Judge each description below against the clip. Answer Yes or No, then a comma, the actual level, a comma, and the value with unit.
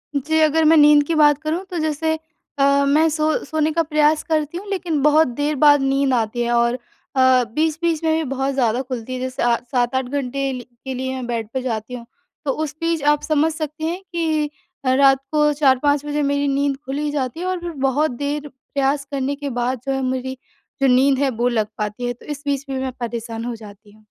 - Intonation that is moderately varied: Yes, average, 3.0 semitones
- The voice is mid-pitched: No, very high, 280 Hz